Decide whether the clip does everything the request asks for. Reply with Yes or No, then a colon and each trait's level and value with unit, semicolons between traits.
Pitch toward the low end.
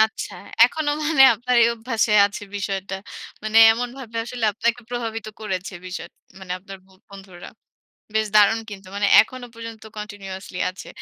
No: high, 220 Hz